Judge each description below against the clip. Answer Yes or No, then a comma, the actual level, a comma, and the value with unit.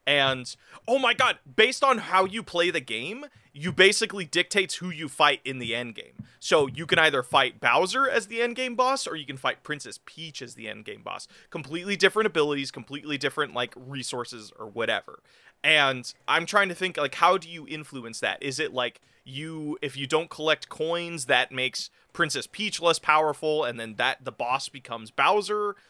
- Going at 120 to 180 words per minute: No, average, 195 wpm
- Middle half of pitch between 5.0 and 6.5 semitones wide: Yes, wide, 5.6 semitones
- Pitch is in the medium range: Yes, medium, 155 Hz